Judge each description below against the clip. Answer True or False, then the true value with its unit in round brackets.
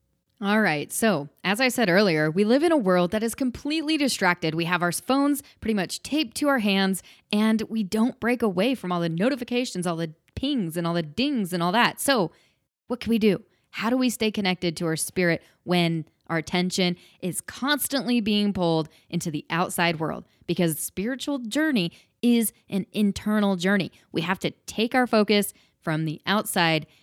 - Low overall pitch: False (200 Hz)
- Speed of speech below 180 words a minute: False (190 wpm)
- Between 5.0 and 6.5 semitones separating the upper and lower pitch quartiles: True (5.6 semitones)